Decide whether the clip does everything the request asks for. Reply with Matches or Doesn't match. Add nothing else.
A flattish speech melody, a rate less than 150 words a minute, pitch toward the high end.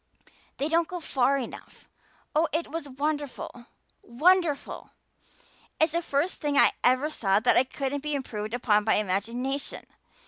Doesn't match